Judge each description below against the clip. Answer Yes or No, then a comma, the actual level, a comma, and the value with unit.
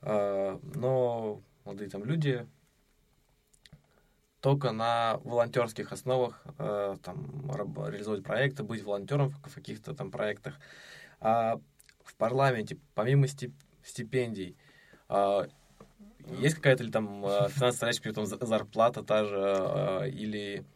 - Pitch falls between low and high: No, low, 115 Hz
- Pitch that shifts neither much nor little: Yes, average, 4.1 semitones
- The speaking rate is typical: No, slow, 100 wpm